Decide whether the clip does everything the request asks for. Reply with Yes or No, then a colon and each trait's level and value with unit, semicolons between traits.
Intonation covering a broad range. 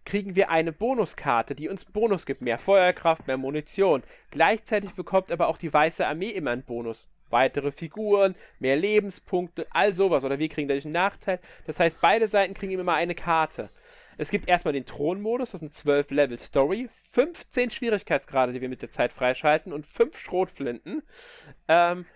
Yes: wide, 5.7 semitones